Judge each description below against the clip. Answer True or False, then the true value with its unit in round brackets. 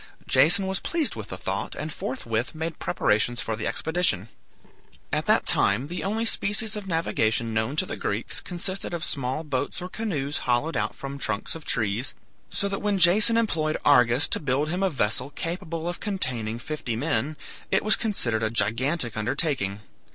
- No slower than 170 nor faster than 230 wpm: True (175 wpm)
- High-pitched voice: False (150 Hz)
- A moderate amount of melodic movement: False (7.3 semitones)